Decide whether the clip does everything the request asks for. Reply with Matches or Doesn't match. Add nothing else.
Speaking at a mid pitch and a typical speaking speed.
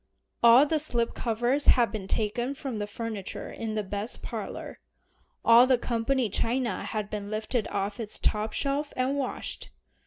Doesn't match